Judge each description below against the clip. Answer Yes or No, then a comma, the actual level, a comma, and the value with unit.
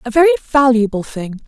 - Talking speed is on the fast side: No, average, 165 wpm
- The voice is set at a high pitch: Yes, very high, 250 Hz